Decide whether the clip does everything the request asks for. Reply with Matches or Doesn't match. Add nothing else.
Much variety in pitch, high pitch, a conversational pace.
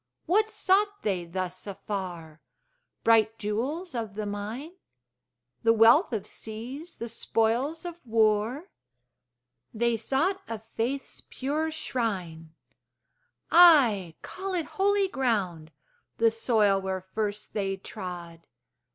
Doesn't match